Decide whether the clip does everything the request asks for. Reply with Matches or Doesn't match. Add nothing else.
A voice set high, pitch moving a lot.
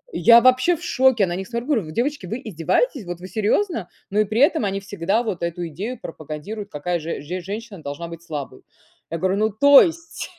Matches